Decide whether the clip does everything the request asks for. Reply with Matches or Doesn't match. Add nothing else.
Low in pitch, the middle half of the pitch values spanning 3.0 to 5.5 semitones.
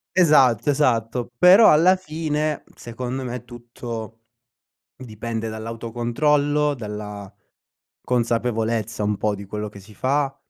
Matches